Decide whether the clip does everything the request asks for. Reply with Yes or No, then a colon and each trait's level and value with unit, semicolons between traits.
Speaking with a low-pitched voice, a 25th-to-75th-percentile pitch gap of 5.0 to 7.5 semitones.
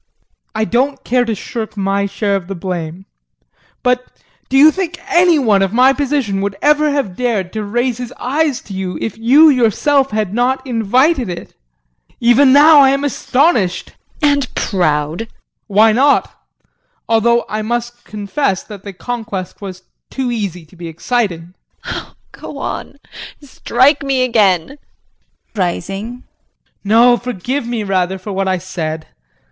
No: high, 230 Hz; average, 5.3 semitones